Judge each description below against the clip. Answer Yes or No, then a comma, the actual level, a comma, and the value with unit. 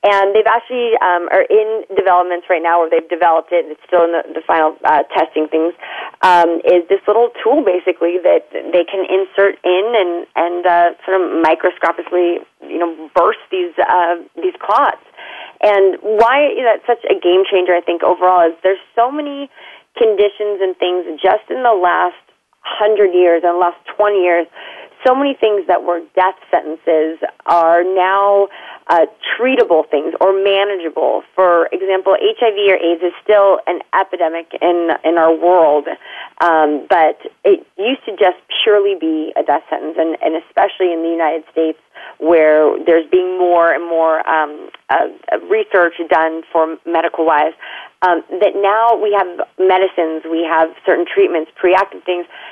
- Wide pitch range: No, average, 3.2 semitones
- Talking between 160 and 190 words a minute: Yes, average, 165 wpm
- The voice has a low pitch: No, medium, 180 Hz